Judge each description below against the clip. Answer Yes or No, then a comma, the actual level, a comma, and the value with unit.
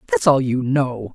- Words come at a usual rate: No, fast, 210 wpm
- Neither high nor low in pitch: No, low, 130 Hz